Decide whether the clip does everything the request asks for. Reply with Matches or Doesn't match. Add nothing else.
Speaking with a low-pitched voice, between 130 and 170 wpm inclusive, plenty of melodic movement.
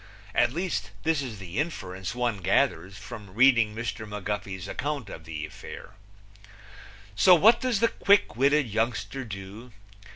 Matches